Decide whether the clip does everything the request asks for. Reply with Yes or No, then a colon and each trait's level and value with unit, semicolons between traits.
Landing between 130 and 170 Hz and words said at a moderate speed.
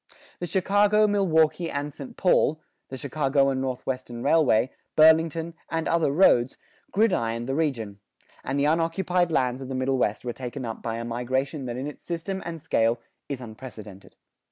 Yes: medium, 140 Hz; average, 165 wpm